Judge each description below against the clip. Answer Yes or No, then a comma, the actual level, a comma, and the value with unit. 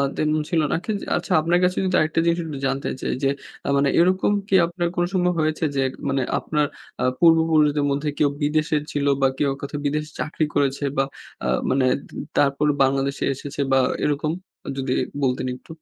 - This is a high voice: No, medium, 150 Hz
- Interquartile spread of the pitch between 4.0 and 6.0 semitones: No, average, 2.8 semitones